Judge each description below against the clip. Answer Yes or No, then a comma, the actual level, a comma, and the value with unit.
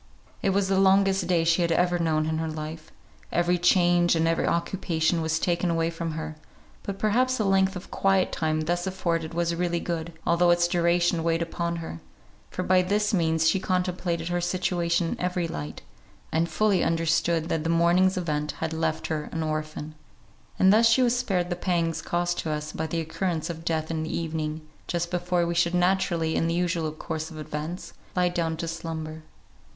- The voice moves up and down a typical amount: No, narrow, 1.9 semitones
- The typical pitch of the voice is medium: Yes, medium, 170 Hz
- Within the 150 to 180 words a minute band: No, average, 195 wpm